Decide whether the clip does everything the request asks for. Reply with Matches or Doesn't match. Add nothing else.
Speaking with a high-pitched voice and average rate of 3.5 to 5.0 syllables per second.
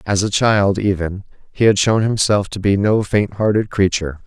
Doesn't match